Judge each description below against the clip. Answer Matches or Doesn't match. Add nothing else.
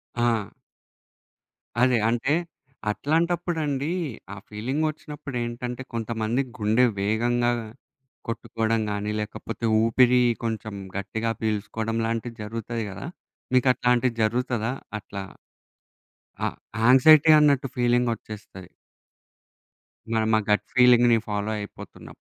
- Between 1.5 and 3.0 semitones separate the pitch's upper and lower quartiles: Matches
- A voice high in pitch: Doesn't match